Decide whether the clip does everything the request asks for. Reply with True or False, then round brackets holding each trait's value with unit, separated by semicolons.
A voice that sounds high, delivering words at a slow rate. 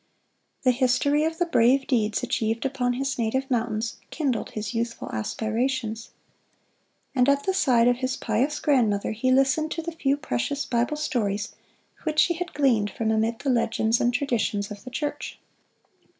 False (250 Hz; 165 wpm)